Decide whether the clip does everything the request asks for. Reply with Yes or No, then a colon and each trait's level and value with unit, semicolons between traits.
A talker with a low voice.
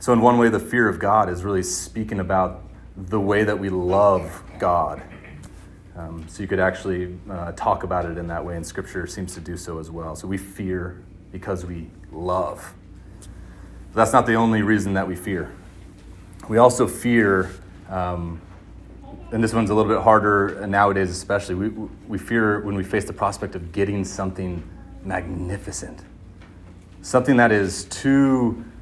Yes: very low, 95 Hz